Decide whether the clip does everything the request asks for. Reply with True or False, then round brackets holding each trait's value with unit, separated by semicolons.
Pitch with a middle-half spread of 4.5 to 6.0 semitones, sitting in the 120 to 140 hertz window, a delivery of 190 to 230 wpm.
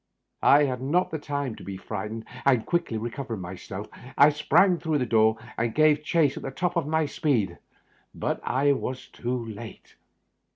False (5.1 semitones; 135 Hz; 180 wpm)